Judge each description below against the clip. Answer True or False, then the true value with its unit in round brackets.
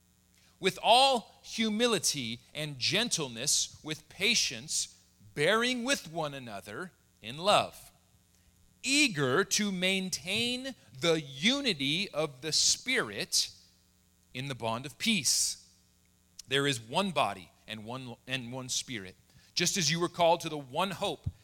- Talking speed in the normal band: False (125 wpm)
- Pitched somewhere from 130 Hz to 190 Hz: True (140 Hz)